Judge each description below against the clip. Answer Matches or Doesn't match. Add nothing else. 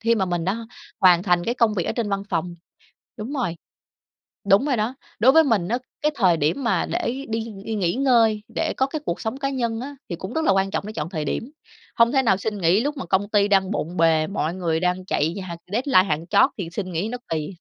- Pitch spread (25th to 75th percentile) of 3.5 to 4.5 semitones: Doesn't match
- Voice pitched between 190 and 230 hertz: Matches